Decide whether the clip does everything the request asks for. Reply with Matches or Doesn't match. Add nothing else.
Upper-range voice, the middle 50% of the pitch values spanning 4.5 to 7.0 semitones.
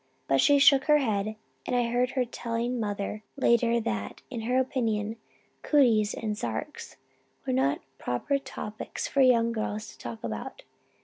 Doesn't match